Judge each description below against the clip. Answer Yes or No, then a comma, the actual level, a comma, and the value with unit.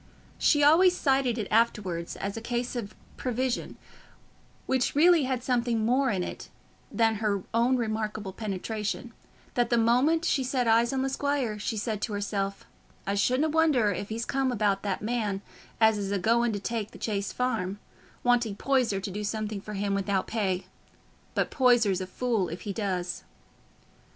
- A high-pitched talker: Yes, high, 225 Hz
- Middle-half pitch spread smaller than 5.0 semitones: Yes, average, 3.7 semitones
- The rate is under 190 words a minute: Yes, average, 170 wpm